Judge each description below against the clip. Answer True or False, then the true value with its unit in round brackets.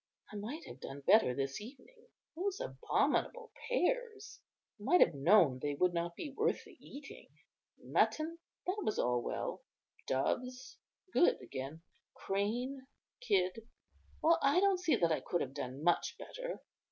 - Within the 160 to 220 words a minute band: False (150 wpm)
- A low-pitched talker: False (235 Hz)